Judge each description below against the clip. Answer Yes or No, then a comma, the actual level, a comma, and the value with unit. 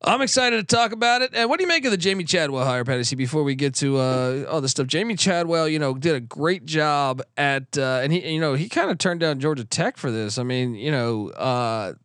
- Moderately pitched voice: Yes, medium, 150 Hz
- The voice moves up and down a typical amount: No, wide, 5.7 semitones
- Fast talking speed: Yes, fast, 265 wpm